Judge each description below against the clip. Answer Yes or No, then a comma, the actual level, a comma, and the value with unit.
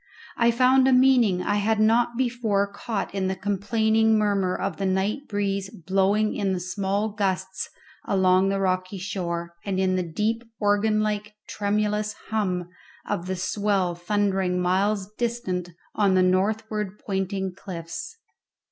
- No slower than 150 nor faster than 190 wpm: No, average, 140 wpm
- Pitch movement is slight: Yes, narrow, 2.3 semitones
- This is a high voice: Yes, high, 200 Hz